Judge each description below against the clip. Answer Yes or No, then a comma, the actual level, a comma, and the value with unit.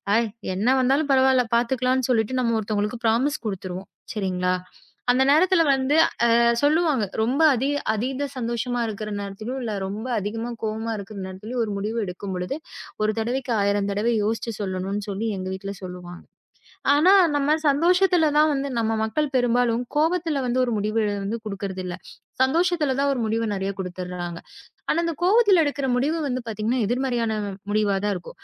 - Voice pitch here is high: Yes, high, 230 Hz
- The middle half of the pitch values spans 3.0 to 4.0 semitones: No, average, 4.8 semitones